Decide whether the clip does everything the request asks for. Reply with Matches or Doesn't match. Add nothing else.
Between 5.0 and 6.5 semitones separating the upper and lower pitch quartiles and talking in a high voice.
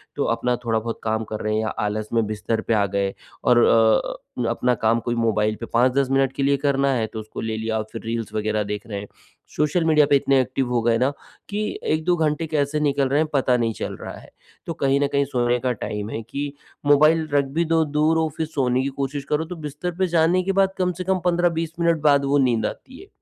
Doesn't match